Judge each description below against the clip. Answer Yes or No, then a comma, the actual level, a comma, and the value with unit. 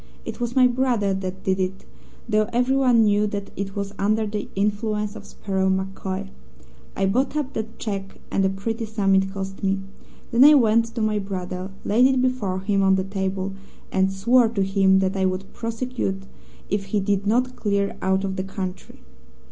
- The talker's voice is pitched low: No, high, 200 Hz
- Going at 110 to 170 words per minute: No, average, 190 wpm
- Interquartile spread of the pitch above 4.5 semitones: No, average, 2.9 semitones